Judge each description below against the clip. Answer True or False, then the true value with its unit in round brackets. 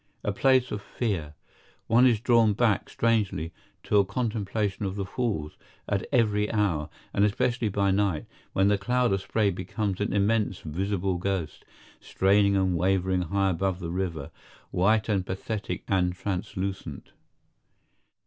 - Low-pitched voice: True (100 Hz)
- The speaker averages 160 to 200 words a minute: False (145 wpm)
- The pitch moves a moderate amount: False (2.3 semitones)